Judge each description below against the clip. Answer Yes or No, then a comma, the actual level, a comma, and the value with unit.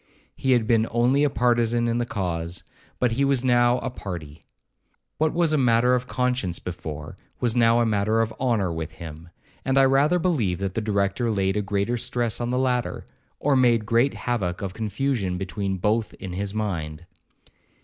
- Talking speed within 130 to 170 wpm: No, average, 190 wpm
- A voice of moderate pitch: No, low, 115 Hz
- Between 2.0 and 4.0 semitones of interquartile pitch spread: No, average, 4.5 semitones